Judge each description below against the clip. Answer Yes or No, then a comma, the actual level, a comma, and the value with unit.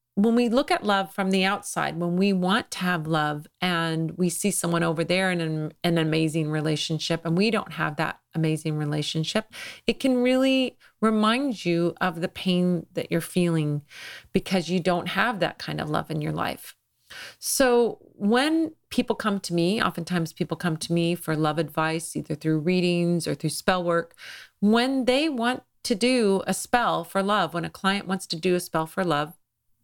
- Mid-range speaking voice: Yes, medium, 180 Hz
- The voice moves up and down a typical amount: Yes, average, 4.4 semitones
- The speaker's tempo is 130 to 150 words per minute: No, average, 185 wpm